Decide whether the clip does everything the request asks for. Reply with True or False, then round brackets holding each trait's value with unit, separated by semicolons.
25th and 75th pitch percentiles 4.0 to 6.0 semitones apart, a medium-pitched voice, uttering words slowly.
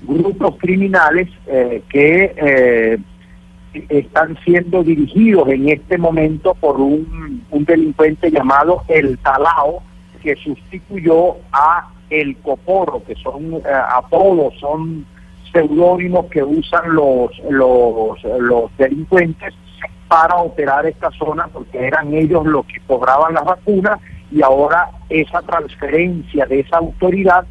True (4.4 semitones; 155 Hz; 120 wpm)